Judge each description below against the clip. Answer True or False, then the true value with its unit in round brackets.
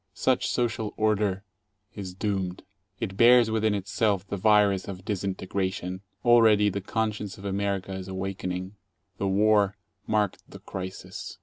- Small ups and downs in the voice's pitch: True (2.1 semitones)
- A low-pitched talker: True (100 Hz)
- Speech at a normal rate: False (130 wpm)